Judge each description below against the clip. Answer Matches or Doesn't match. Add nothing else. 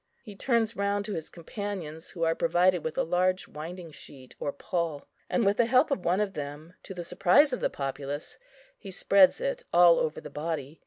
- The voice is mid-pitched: Matches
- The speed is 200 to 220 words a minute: Matches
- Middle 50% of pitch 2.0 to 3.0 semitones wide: Doesn't match